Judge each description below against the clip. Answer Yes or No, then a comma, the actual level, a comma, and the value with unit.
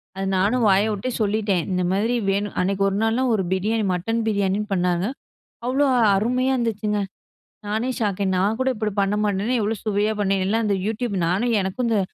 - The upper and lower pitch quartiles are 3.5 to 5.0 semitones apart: No, narrow, 2.5 semitones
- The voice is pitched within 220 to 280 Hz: No, high, 210 Hz